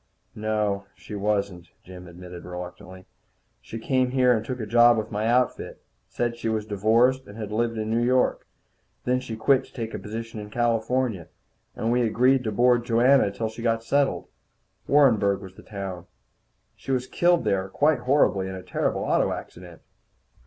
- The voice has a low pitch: Yes, low, 110 Hz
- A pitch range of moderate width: Yes, average, 3.8 semitones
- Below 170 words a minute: No, average, 175 wpm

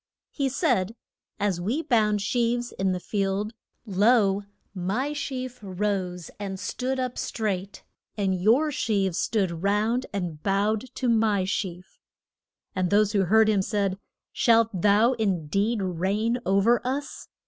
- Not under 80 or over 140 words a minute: Yes, slow, 135 wpm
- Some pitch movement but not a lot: Yes, average, 3.4 semitones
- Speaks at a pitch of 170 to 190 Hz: No, high, 205 Hz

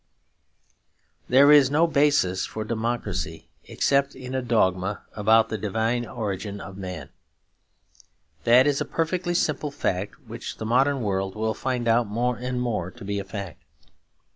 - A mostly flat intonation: No, average, 4.6 semitones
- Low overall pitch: Yes, low, 115 Hz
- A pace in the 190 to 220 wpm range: No, average, 150 wpm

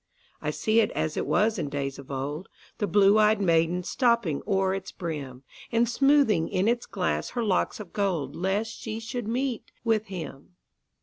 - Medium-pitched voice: No, high, 195 Hz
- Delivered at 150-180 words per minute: Yes, average, 165 wpm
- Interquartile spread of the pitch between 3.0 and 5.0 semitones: No, wide, 5.4 semitones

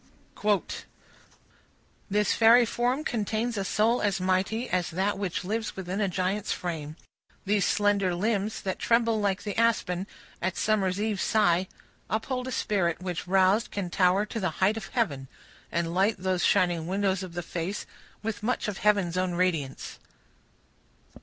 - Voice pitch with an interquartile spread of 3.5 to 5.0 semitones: No, average, 2.9 semitones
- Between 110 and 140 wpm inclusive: No, average, 160 wpm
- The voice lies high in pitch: Yes, high, 195 Hz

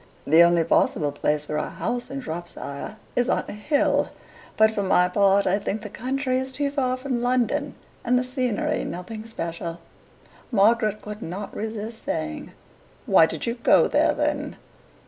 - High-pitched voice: Yes, high, 215 Hz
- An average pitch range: No, wide, 6.2 semitones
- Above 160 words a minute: Yes, average, 170 wpm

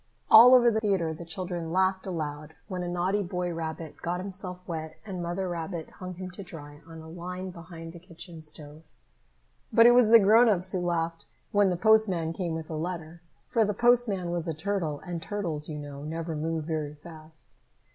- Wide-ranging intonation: No, average, 2.9 semitones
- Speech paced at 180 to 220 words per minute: Yes, average, 195 wpm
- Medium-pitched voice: Yes, medium, 175 Hz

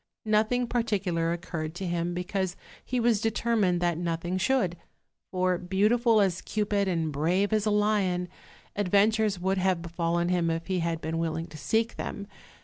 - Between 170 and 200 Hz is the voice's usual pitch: Yes, medium, 185 Hz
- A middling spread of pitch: Yes, average, 3.7 semitones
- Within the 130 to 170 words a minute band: Yes, average, 160 wpm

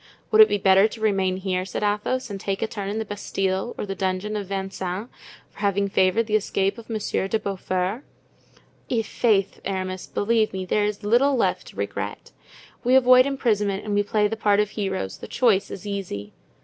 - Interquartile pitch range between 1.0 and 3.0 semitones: Yes, narrow, 2.4 semitones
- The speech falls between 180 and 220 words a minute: Yes, average, 195 wpm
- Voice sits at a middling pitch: No, high, 205 Hz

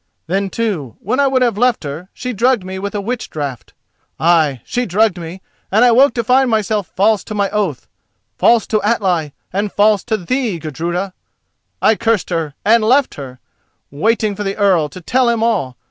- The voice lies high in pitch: Yes, high, 205 Hz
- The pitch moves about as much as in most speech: Yes, average, 5.0 semitones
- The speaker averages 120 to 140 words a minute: No, average, 190 wpm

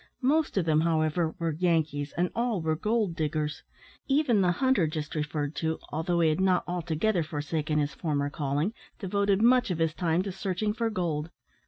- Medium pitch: Yes, medium, 170 Hz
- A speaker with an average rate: Yes, average, 180 wpm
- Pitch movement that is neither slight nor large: Yes, average, 4.2 semitones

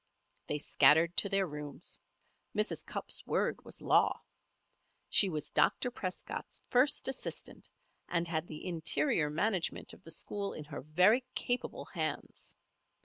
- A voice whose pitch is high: No, medium, 175 Hz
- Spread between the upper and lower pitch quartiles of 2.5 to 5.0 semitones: No, wide, 5.5 semitones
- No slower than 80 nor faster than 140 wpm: Yes, slow, 135 wpm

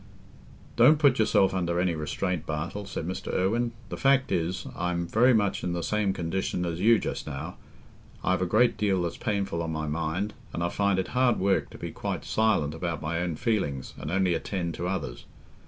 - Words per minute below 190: No, average, 200 wpm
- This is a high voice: No, very low, 90 Hz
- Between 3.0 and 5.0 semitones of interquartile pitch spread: Yes, average, 3.7 semitones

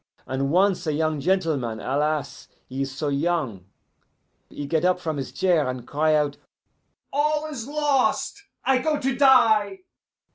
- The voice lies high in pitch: No, medium, 160 Hz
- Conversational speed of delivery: Yes, average, 150 wpm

